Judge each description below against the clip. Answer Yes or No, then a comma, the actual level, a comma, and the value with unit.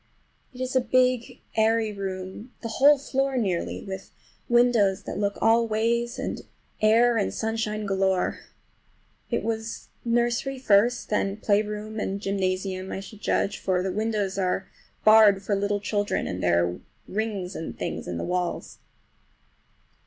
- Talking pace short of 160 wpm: Yes, average, 150 wpm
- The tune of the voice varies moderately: Yes, average, 3.1 semitones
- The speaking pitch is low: No, high, 210 Hz